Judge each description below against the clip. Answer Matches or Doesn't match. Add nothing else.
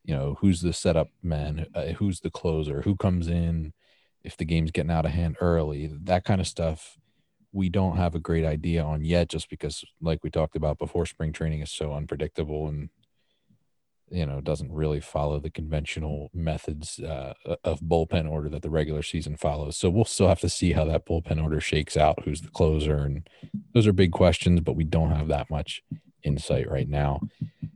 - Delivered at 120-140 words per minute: Doesn't match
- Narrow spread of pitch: Matches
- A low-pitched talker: Matches